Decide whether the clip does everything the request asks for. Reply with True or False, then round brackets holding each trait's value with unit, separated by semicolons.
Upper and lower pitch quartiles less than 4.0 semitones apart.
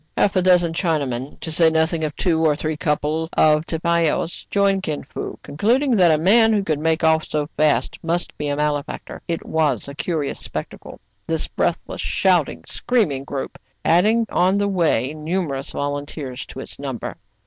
True (3.3 semitones)